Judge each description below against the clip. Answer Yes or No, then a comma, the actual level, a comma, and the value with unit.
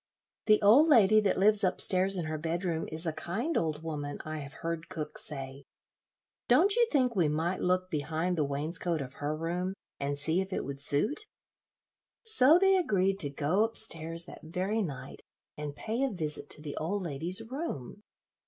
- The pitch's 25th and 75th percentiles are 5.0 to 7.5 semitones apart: Yes, average, 5.3 semitones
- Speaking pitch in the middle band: Yes, medium, 170 Hz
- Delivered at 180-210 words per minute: Yes, average, 185 wpm